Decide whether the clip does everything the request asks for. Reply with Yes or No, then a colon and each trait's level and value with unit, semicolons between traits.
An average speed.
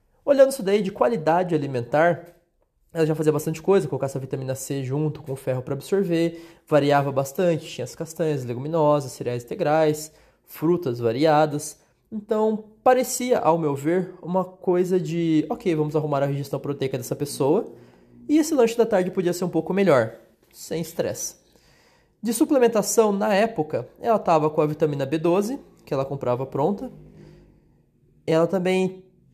Yes: average, 155 wpm